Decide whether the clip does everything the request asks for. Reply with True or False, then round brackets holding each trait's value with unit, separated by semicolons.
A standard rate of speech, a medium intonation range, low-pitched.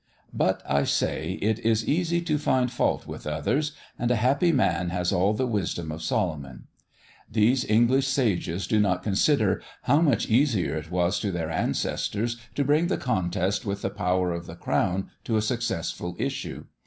False (175 wpm; 6.1 semitones; 105 Hz)